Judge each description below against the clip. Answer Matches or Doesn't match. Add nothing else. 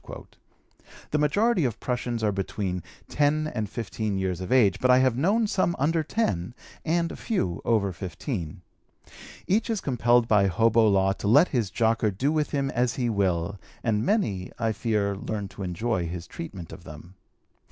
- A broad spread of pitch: Matches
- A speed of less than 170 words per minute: Doesn't match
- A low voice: Matches